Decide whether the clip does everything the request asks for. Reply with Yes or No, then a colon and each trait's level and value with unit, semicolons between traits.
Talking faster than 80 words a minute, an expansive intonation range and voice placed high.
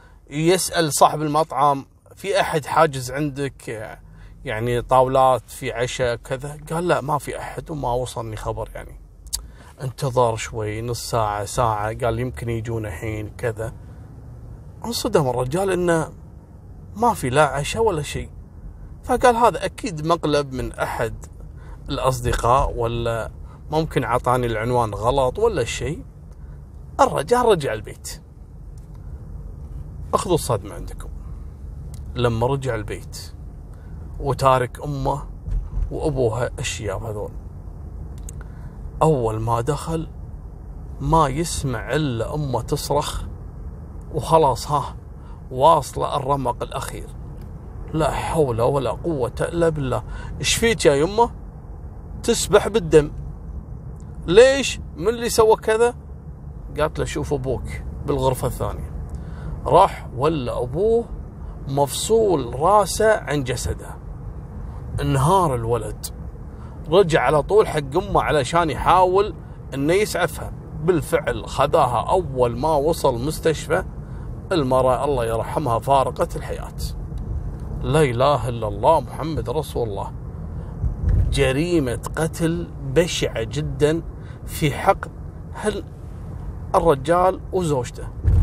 No: average, 100 wpm; wide, 8.6 semitones; low, 125 Hz